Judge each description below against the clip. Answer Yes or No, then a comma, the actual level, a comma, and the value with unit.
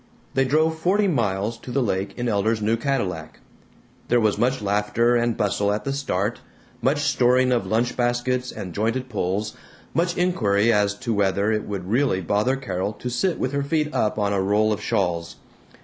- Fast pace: No, average, 185 wpm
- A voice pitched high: No, low, 115 Hz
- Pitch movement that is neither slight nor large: Yes, average, 4.2 semitones